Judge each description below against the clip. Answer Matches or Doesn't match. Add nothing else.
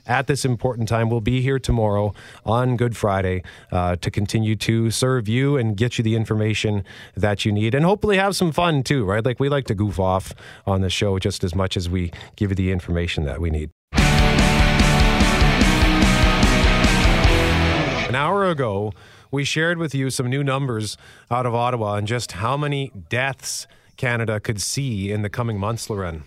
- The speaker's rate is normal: Matches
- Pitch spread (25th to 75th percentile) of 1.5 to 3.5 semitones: Doesn't match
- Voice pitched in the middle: Doesn't match